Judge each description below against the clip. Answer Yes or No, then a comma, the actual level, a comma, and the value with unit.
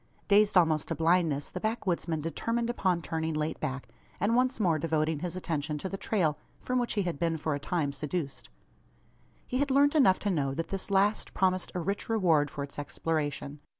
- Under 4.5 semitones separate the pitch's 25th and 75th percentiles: No, average, 4.8 semitones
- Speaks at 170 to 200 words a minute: Yes, average, 195 wpm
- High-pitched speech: No, medium, 170 Hz